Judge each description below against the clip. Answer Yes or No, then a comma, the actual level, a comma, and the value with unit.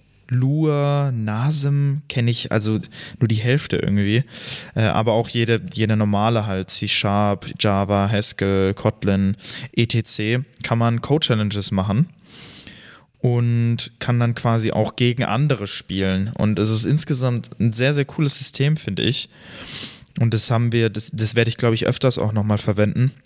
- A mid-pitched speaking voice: No, low, 115 Hz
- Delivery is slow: No, average, 155 wpm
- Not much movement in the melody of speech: No, average, 3.6 semitones